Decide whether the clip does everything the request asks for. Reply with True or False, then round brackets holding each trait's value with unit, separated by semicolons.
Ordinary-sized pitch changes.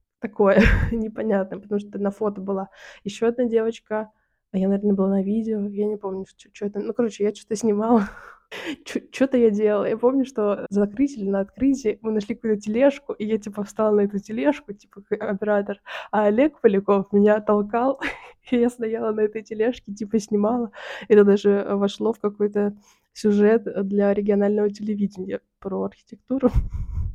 False (2.0 semitones)